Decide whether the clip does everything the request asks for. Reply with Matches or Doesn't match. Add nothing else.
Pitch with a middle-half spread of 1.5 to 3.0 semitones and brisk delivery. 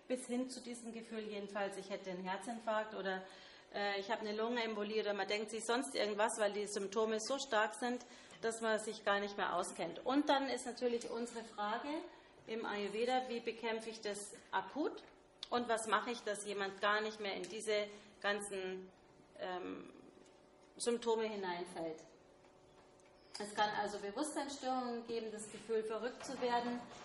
Doesn't match